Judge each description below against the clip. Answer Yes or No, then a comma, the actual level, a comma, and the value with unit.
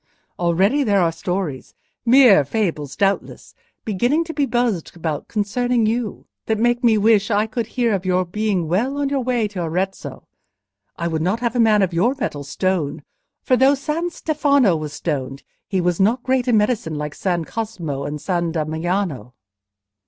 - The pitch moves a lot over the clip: Yes, wide, 6.1 semitones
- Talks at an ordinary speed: Yes, average, 165 wpm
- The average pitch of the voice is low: No, high, 200 Hz